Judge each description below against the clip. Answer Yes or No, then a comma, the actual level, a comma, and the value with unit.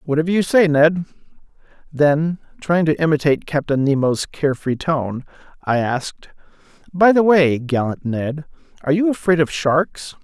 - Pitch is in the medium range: Yes, medium, 155 Hz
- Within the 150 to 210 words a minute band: No, average, 140 wpm